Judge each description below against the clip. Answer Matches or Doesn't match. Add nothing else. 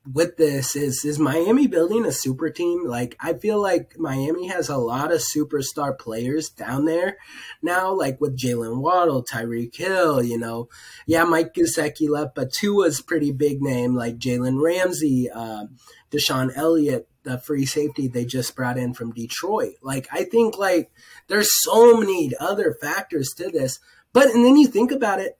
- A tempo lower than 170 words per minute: Doesn't match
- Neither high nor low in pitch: Matches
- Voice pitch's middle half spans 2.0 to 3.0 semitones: Doesn't match